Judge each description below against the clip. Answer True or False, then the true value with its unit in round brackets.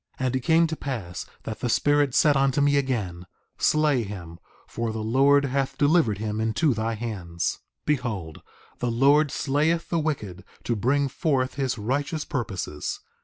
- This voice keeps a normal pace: True (170 wpm)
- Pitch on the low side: True (130 Hz)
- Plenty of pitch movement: False (4.7 semitones)